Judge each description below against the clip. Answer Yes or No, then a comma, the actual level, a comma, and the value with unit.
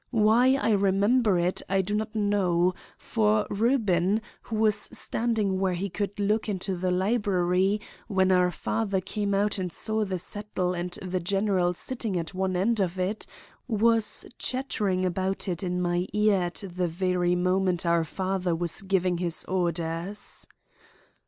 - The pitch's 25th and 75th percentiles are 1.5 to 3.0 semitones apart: Yes, narrow, 2.6 semitones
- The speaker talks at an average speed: Yes, average, 155 wpm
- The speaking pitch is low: No, high, 190 Hz